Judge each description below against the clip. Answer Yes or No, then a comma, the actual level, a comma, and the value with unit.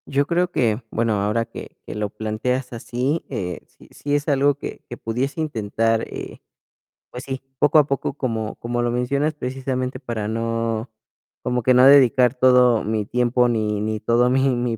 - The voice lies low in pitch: Yes, low, 125 Hz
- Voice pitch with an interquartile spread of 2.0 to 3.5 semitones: Yes, average, 3.0 semitones